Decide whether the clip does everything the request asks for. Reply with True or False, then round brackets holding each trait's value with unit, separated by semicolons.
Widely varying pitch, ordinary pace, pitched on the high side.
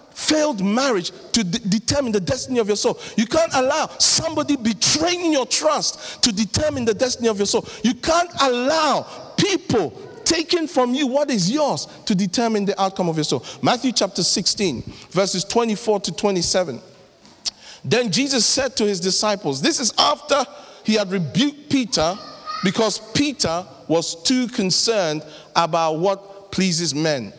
True (6.4 semitones; 155 wpm; 225 Hz)